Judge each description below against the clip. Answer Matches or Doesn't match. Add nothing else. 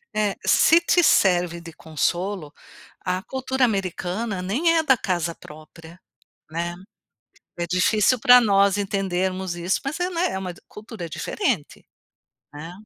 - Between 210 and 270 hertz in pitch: Doesn't match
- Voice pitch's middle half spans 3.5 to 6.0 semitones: Matches